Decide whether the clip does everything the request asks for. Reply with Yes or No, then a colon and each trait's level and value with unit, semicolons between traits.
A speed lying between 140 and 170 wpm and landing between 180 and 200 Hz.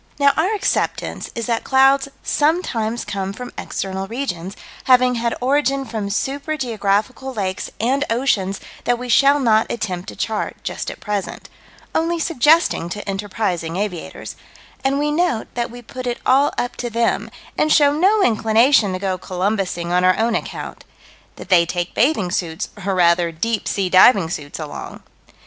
No: average, 165 wpm; high, 225 Hz